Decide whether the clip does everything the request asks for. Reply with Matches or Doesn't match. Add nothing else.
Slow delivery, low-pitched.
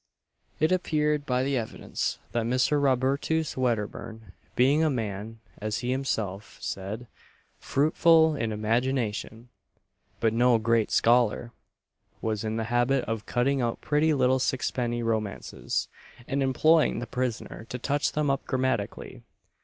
Matches